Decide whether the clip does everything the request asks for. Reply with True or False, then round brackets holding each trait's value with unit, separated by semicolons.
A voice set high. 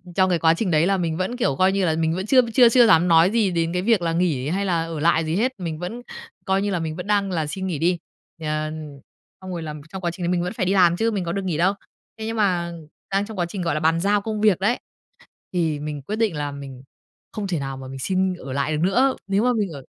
False (180 Hz)